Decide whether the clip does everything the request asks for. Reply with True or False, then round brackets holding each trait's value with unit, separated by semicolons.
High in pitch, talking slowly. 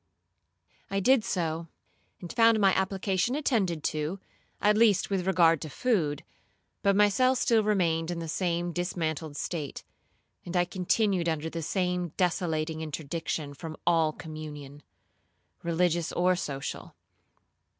False (175 Hz; 130 wpm)